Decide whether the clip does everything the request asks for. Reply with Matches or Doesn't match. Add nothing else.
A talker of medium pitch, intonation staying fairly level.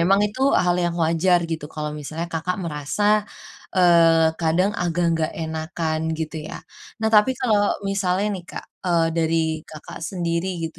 Matches